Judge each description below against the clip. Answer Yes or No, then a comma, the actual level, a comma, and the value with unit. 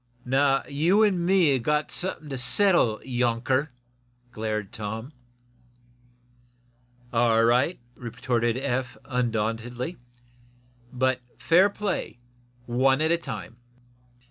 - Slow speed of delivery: Yes, slow, 100 wpm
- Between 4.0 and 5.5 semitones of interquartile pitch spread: Yes, average, 4.5 semitones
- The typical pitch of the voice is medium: No, low, 130 Hz